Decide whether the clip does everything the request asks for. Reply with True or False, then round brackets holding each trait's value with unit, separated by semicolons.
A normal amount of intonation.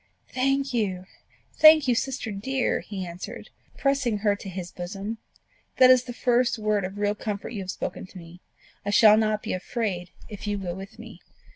True (4.1 semitones)